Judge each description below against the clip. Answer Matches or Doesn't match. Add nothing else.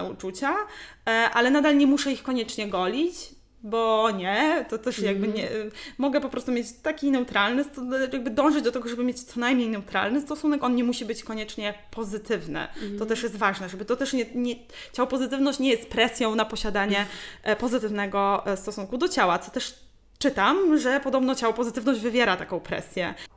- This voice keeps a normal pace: Doesn't match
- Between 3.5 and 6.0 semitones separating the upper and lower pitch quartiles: Matches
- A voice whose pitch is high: Matches